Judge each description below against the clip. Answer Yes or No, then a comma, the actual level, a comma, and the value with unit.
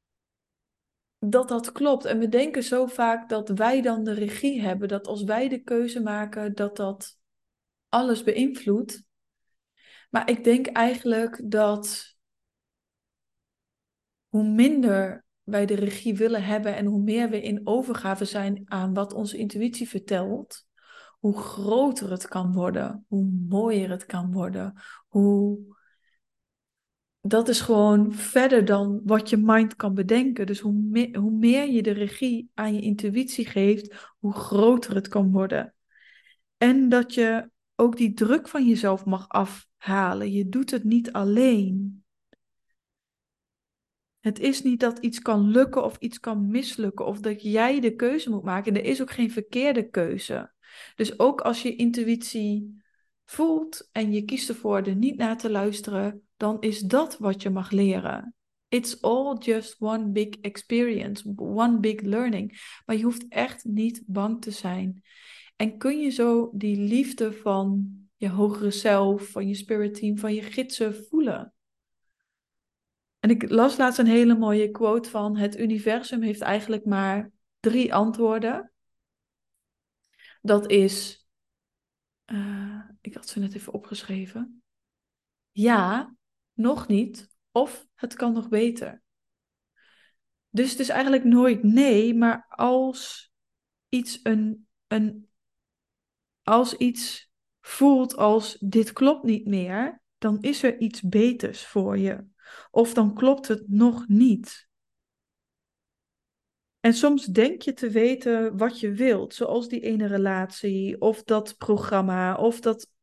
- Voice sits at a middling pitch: No, high, 220 Hz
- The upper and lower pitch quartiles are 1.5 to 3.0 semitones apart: Yes, average, 2.7 semitones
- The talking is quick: No, average, 140 wpm